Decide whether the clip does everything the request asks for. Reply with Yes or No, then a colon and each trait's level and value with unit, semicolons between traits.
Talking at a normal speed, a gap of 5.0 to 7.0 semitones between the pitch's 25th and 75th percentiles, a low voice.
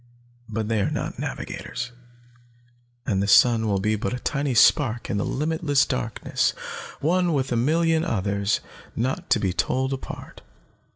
Yes: average, 155 wpm; average, 5.3 semitones; low, 125 Hz